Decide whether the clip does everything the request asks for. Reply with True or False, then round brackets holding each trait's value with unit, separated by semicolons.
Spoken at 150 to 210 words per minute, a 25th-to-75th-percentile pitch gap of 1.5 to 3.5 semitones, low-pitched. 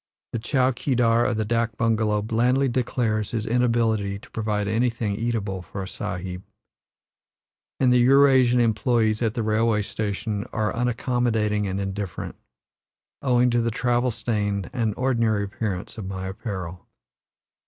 False (140 wpm; 2.8 semitones; 110 Hz)